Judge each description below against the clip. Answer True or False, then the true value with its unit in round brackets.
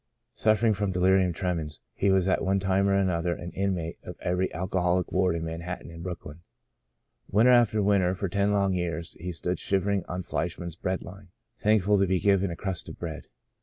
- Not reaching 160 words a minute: False (190 wpm)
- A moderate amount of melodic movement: False (2.1 semitones)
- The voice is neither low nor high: False (95 Hz)